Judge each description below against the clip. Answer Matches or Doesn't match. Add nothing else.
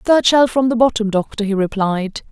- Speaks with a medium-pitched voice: Doesn't match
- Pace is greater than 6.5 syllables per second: Doesn't match